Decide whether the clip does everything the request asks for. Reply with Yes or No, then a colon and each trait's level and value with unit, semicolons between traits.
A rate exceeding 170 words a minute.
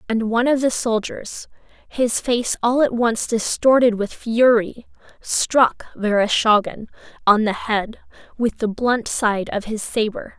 No: average, 145 wpm